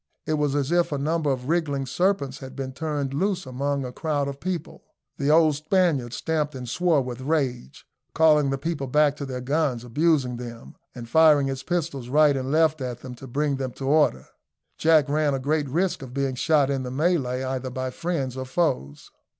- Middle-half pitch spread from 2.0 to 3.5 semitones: Yes, average, 3.2 semitones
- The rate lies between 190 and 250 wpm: Yes, average, 200 wpm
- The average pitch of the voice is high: No, medium, 140 Hz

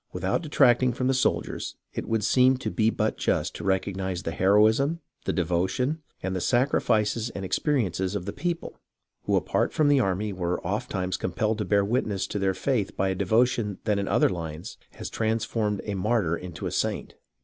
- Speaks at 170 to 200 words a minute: Yes, average, 185 wpm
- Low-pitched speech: Yes, low, 105 Hz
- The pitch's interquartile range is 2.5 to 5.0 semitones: Yes, average, 4.4 semitones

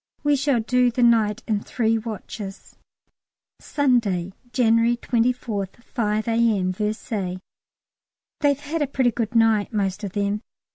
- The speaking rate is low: Yes, slow, 130 wpm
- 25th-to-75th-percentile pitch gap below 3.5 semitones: Yes, average, 2.9 semitones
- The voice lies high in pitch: Yes, high, 225 Hz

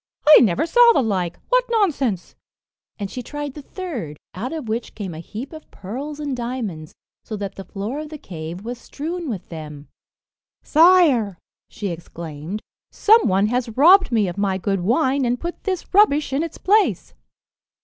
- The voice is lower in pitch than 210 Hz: No, high, 245 Hz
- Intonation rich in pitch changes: Yes, wide, 8.0 semitones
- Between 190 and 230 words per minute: No, average, 175 wpm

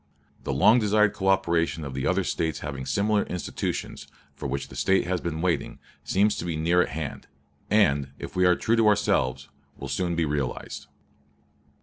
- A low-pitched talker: Yes, very low, 85 Hz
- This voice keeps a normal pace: Yes, average, 180 wpm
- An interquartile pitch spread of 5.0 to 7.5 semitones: Yes, wide, 5.5 semitones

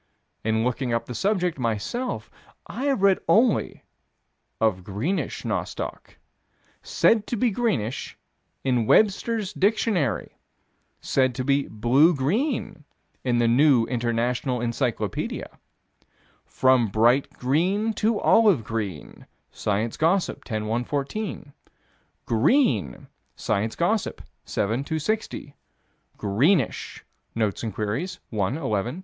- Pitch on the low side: Yes, low, 130 Hz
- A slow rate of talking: Yes, slow, 105 wpm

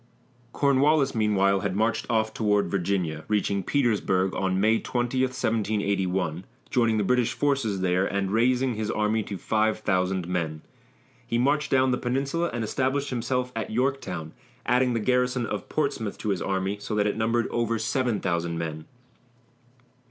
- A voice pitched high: No, low, 110 Hz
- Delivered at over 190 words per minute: No, average, 150 wpm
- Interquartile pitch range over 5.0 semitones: No, average, 4.4 semitones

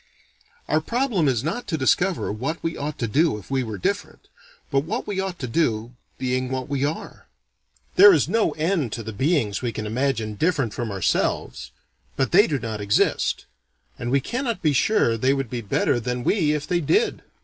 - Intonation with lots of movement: Yes, wide, 6.2 semitones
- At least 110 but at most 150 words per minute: No, average, 195 wpm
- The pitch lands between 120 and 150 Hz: Yes, low, 135 Hz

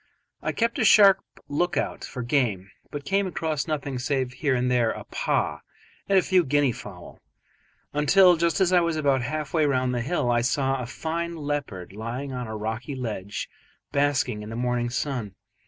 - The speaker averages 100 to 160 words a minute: No, average, 190 wpm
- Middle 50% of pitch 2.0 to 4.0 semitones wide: No, average, 4.7 semitones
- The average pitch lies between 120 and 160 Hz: Yes, low, 135 Hz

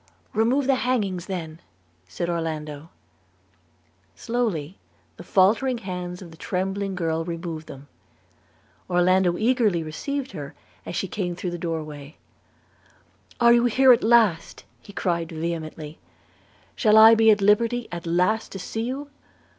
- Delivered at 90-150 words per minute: Yes, average, 140 wpm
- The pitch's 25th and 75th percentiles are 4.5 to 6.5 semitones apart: Yes, average, 5.3 semitones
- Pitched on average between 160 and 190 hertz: Yes, medium, 185 Hz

